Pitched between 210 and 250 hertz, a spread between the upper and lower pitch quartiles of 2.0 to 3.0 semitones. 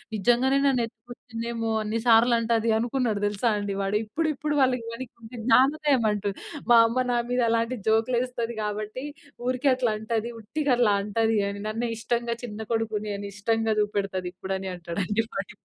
Yes: high, 230 Hz; narrow, 2.6 semitones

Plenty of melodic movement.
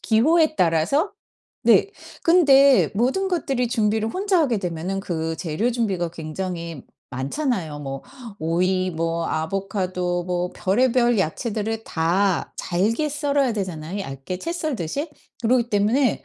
Yes: wide, 7.1 semitones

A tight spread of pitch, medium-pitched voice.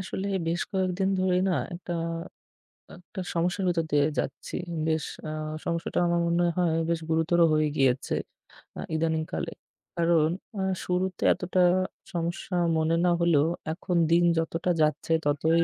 Yes: narrow, 2.1 semitones; medium, 170 Hz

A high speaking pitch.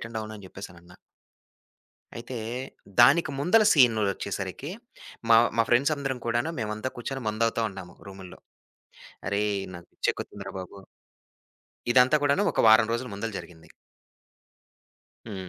No: low, 110 Hz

